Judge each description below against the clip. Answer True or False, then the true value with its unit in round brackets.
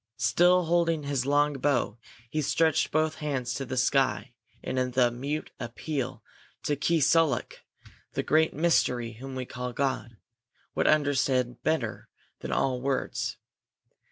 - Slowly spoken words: True (130 wpm)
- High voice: False (135 Hz)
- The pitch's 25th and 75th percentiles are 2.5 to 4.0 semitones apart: True (3.5 semitones)